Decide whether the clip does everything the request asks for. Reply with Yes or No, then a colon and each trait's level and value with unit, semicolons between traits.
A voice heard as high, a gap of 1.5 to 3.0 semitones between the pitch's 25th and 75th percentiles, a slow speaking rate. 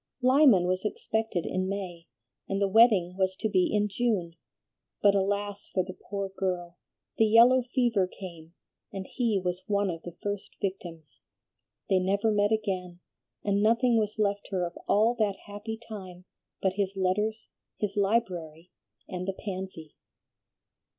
No: high, 195 Hz; average, 2.7 semitones; average, 150 wpm